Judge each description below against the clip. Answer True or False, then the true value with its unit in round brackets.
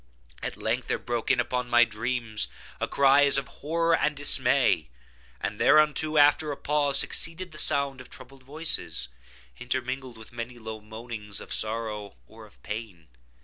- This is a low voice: True (125 Hz)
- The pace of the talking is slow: False (160 wpm)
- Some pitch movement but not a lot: True (4.4 semitones)